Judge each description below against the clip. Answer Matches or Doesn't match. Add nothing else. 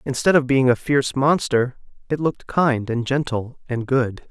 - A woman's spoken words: Doesn't match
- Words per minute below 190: Matches